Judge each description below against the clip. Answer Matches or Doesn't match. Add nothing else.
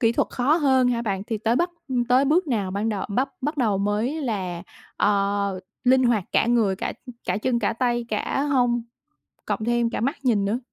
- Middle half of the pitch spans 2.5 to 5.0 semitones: Matches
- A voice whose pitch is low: Doesn't match